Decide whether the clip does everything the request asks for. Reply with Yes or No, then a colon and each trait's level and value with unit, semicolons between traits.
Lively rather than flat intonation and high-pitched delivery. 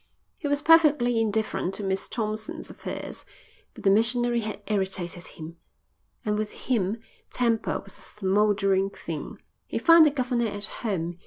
No: average, 3.7 semitones; high, 215 Hz